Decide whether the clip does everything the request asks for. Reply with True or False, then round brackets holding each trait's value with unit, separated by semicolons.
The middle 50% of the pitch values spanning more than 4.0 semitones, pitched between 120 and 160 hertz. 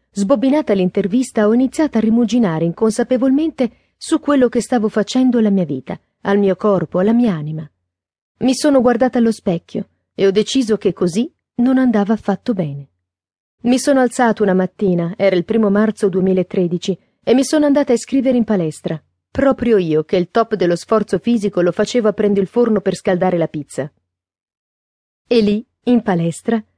False (5.1 semitones; 210 Hz)